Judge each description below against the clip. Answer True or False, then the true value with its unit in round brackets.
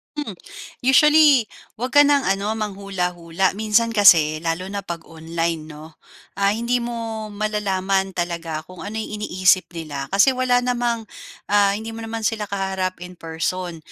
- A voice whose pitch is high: True (200 Hz)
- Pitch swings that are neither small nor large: True (4.5 semitones)